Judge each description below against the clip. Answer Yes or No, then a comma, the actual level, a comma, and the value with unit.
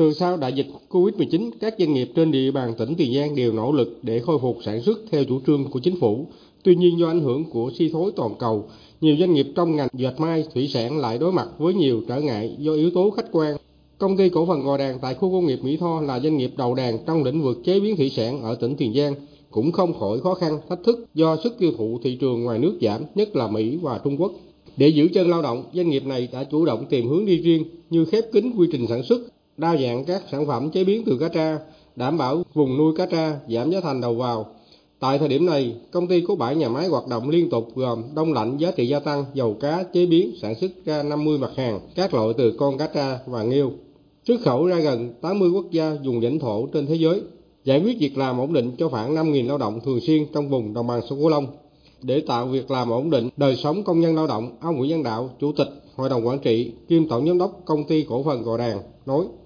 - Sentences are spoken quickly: Yes, fast, 260 wpm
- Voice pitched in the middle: Yes, medium, 150 Hz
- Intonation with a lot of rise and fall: No, average, 4.8 semitones